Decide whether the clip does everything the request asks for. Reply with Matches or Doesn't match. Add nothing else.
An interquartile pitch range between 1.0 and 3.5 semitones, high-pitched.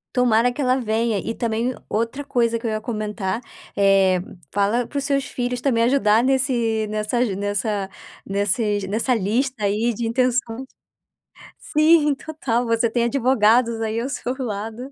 Matches